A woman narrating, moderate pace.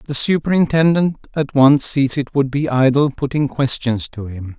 No: male; average, 170 wpm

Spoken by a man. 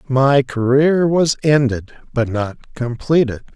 Yes: male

